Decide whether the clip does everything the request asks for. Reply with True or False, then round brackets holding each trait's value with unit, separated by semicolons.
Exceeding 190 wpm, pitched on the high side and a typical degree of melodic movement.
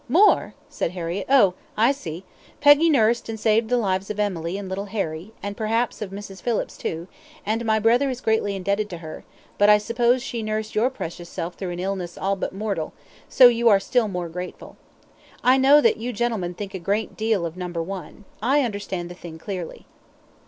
True (200 wpm; 205 Hz; 4.1 semitones)